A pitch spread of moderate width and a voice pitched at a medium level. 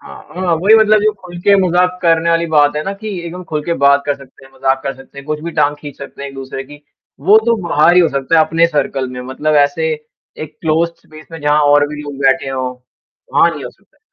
Yes: average, 3.4 semitones; medium, 150 Hz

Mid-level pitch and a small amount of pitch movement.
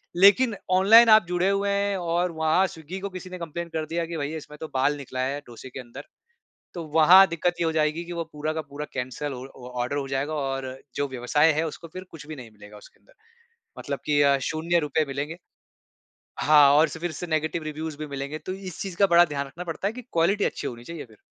No: medium, 155 Hz; average, 3.7 semitones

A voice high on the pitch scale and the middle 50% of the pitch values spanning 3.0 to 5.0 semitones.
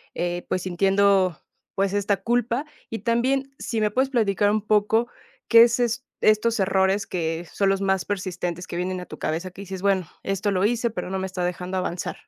Yes: high, 195 Hz; average, 3.3 semitones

